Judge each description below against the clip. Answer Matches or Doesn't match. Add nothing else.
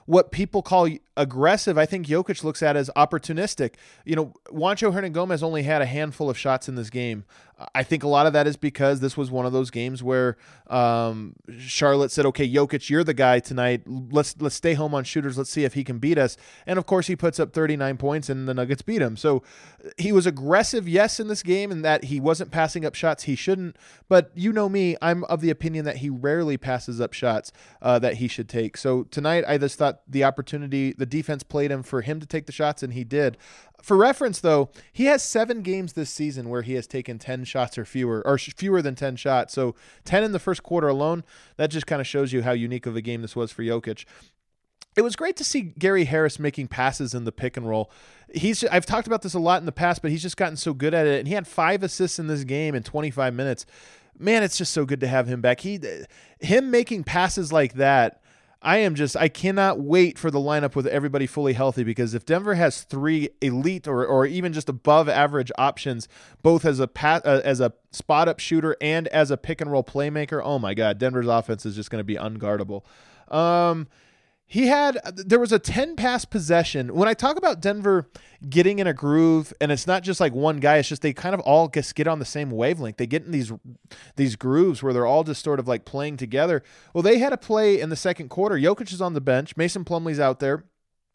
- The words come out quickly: Matches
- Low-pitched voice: Doesn't match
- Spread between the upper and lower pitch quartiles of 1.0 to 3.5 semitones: Doesn't match